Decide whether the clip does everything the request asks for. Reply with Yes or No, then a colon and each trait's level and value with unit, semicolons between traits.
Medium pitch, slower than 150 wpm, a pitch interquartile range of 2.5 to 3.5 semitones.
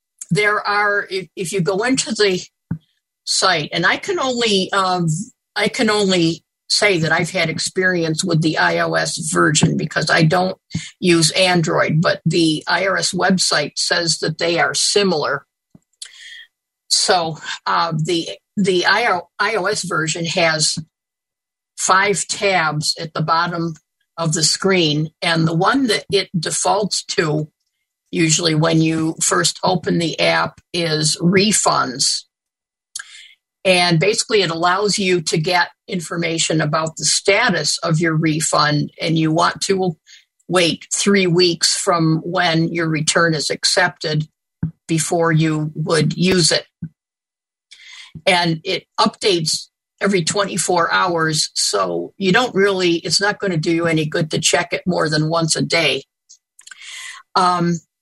Yes: medium, 175 Hz; slow, 135 wpm; average, 2.8 semitones